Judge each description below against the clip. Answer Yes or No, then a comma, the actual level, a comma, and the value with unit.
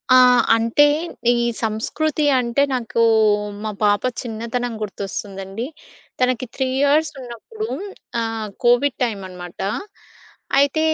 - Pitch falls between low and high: No, high, 235 Hz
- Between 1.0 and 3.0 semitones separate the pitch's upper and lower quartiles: No, average, 3.7 semitones